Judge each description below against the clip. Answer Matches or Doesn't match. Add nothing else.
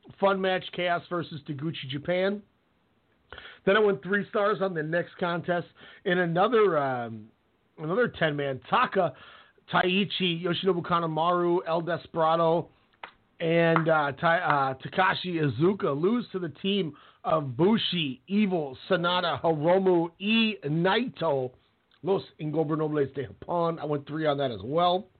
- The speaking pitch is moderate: Matches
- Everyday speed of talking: Doesn't match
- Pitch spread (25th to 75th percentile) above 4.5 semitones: Doesn't match